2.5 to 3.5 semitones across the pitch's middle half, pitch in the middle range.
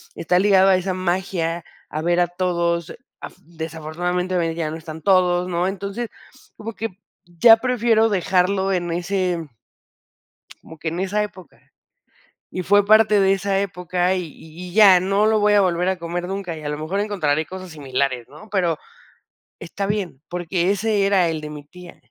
Yes: average, 2.8 semitones; medium, 180 Hz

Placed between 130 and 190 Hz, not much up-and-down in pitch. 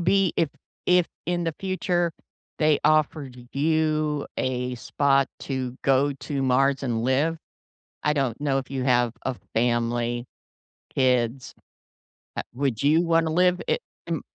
No: medium, 140 Hz; average, 3.9 semitones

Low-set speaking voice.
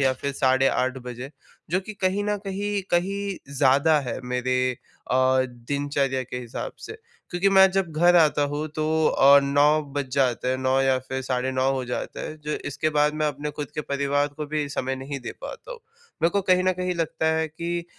No: medium, 145 Hz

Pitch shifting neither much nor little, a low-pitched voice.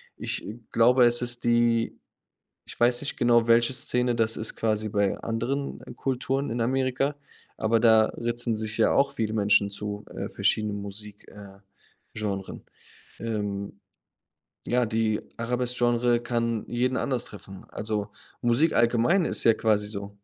No: narrow, 2.3 semitones; low, 115 Hz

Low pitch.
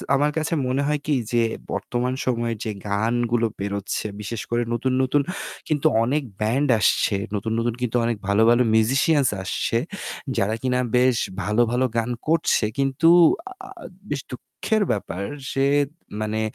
Yes: low, 120 Hz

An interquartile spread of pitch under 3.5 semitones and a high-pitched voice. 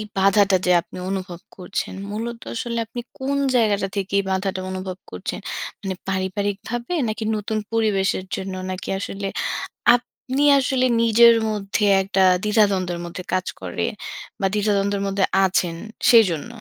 Yes: average, 2.8 semitones; high, 200 Hz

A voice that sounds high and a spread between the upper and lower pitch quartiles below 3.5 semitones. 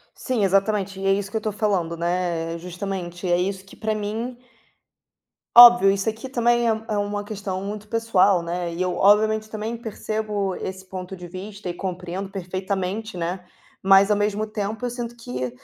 Yes: high, 200 Hz; average, 2.9 semitones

